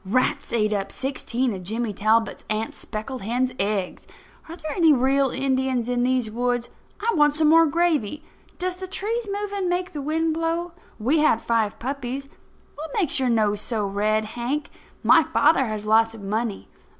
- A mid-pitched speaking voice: No, very high, 255 Hz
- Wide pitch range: Yes, wide, 6.0 semitones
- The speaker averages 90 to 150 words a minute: No, average, 175 wpm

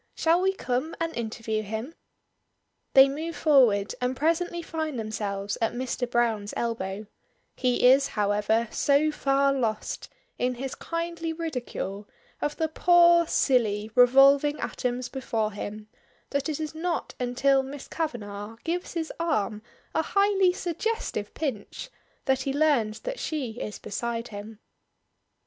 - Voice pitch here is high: Yes, very high, 260 Hz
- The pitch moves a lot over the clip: Yes, wide, 6.3 semitones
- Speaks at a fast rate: No, slow, 135 wpm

